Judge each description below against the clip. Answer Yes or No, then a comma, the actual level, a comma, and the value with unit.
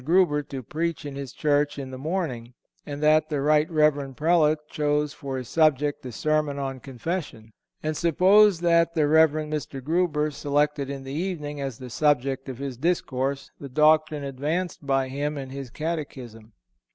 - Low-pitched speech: No, medium, 145 Hz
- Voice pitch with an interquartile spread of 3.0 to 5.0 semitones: No, narrow, 2.4 semitones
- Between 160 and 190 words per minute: Yes, average, 170 wpm